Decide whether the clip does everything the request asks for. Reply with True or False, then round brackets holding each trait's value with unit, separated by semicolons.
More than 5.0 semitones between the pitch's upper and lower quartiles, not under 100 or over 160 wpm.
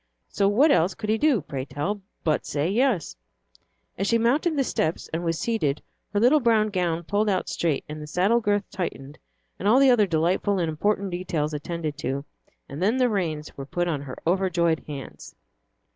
False (5.4 semitones; 190 wpm)